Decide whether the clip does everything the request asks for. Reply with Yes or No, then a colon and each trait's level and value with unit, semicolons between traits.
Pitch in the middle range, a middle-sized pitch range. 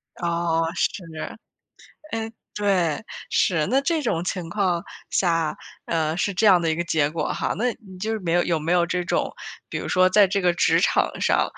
Yes: medium, 175 Hz; average, 3.1 semitones